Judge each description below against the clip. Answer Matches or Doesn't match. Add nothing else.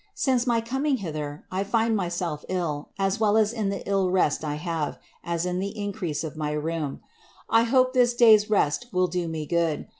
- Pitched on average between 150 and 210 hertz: Matches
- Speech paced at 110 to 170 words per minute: Doesn't match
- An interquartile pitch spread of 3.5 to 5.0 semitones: Doesn't match